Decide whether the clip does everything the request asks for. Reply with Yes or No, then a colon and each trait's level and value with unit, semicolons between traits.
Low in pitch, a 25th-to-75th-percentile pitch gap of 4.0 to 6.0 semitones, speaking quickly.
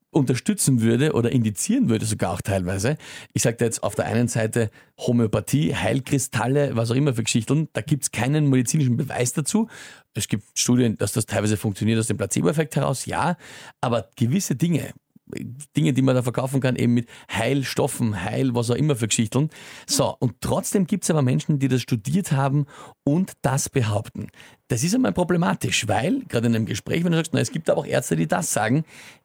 Yes: low, 130 Hz; average, 4.3 semitones; fast, 195 wpm